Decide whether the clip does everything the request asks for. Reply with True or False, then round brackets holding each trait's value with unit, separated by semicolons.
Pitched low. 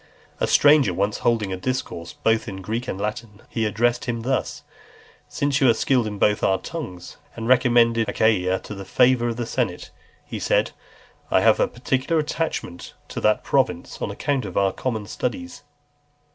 True (115 Hz)